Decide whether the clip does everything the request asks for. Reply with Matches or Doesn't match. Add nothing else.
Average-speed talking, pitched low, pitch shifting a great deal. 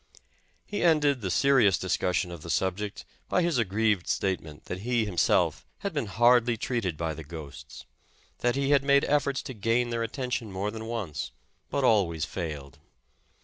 Matches